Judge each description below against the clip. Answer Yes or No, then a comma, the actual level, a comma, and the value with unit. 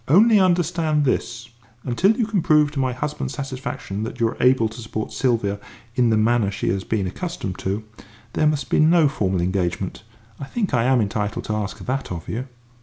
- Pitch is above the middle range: No, low, 125 Hz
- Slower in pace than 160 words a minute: No, average, 195 wpm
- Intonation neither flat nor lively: No, wide, 6.1 semitones